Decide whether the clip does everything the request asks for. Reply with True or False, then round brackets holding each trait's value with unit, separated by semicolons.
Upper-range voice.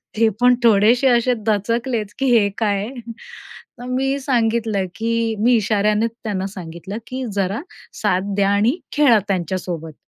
True (220 Hz)